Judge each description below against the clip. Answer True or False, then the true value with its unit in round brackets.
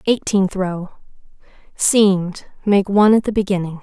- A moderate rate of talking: False (110 wpm)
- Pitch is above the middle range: True (195 Hz)